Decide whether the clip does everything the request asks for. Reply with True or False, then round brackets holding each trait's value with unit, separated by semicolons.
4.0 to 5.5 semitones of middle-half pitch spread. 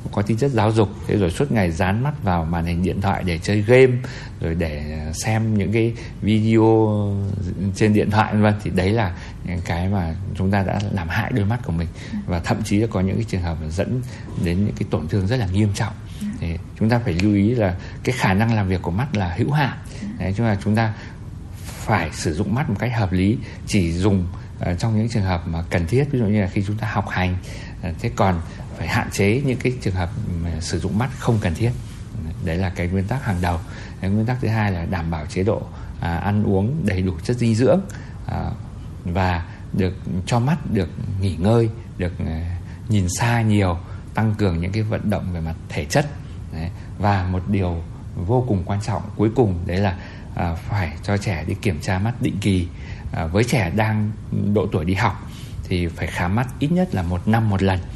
False (3.3 semitones)